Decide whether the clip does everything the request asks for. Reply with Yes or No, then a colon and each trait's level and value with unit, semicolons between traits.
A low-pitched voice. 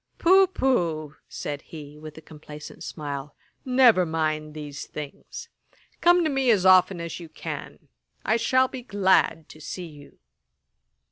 No: medium, 165 Hz